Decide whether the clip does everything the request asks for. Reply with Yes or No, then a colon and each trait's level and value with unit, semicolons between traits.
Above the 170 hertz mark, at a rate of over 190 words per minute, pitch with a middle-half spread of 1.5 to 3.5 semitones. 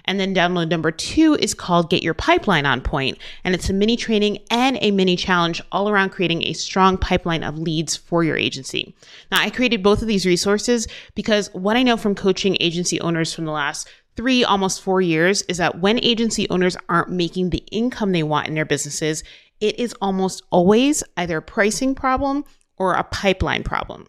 No: high, 190 Hz; average, 200 wpm; average, 3.9 semitones